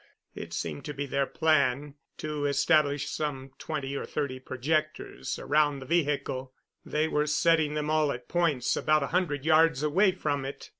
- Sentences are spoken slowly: No, average, 165 wpm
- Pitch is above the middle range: No, medium, 150 Hz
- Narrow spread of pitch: Yes, narrow, 2.1 semitones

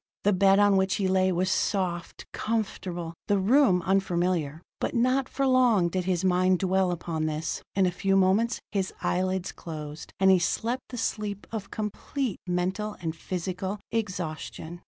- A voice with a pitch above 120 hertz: Yes, high, 190 Hz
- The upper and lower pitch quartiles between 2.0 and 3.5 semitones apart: Yes, narrow, 2.6 semitones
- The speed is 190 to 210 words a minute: No, average, 160 wpm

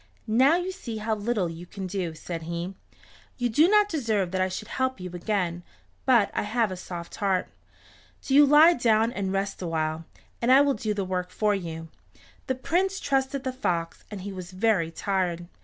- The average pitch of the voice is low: No, high, 205 Hz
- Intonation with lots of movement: Yes, wide, 6.1 semitones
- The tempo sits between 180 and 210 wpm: Yes, average, 195 wpm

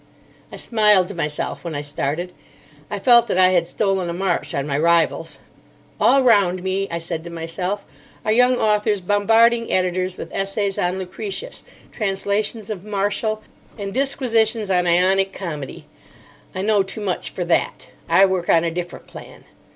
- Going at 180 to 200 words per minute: No, average, 165 wpm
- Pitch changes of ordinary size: Yes, average, 3.3 semitones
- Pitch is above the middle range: Yes, high, 195 Hz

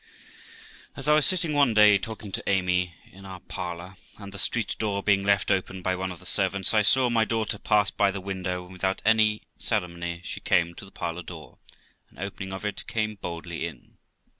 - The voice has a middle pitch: No, very low, 95 Hz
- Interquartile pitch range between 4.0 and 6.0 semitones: No, average, 2.7 semitones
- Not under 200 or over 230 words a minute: Yes, fast, 205 wpm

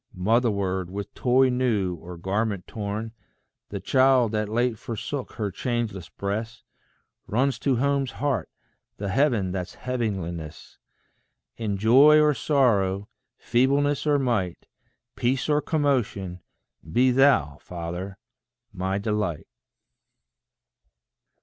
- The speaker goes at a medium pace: No, slow, 105 wpm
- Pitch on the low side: Yes, low, 110 Hz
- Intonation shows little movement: No, average, 5.2 semitones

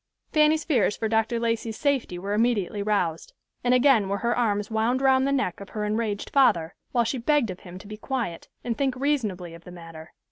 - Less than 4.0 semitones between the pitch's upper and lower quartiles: No, average, 4.4 semitones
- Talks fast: Yes, fast, 210 wpm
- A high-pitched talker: Yes, high, 225 Hz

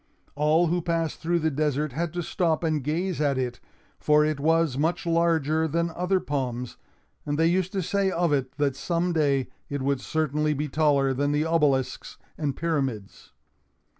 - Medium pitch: Yes, medium, 155 Hz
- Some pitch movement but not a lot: Yes, average, 3.0 semitones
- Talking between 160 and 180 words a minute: Yes, average, 175 wpm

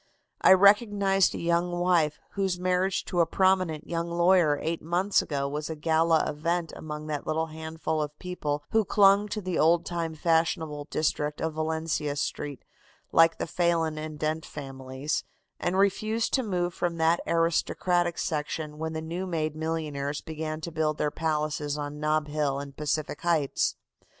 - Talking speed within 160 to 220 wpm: Yes, average, 165 wpm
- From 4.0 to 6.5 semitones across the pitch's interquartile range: No, narrow, 2.6 semitones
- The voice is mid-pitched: Yes, medium, 160 Hz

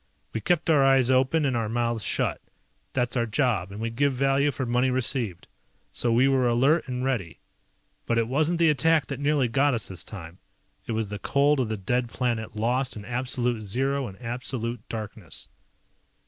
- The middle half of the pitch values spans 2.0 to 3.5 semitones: Yes, average, 3.2 semitones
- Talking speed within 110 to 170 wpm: No, average, 190 wpm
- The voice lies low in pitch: Yes, low, 125 Hz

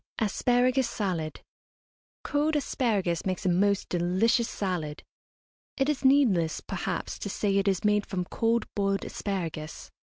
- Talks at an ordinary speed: No, slow, 130 wpm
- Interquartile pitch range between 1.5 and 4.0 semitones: No, average, 4.7 semitones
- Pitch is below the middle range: No, high, 200 Hz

